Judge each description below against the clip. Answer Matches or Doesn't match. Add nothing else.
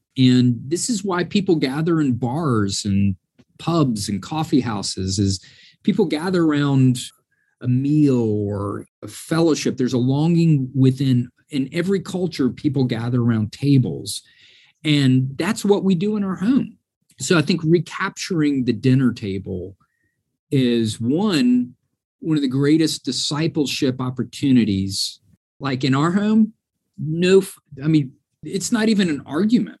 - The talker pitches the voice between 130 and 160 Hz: Matches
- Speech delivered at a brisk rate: Doesn't match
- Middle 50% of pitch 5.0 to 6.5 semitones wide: Matches